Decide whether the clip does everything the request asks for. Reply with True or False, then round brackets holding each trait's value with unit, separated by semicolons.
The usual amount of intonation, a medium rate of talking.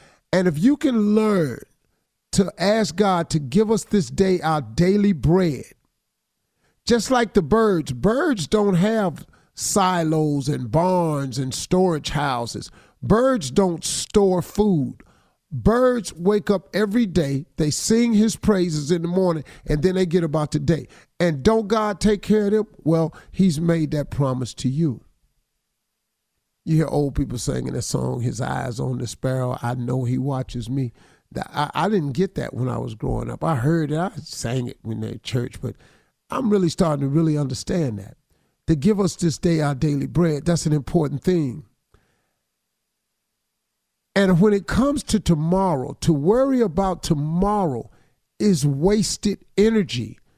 False (6.2 semitones; 160 wpm)